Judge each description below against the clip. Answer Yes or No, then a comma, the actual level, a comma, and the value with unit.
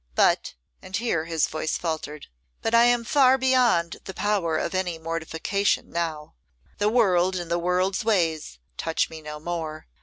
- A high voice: No, medium, 175 Hz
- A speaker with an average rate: Yes, average, 160 wpm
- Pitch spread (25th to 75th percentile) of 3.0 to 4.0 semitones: No, average, 4.4 semitones